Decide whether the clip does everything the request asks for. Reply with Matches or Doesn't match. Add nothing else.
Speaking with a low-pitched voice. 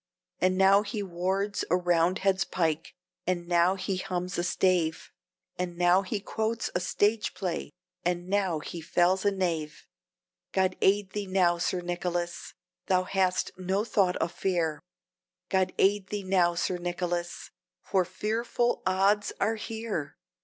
Doesn't match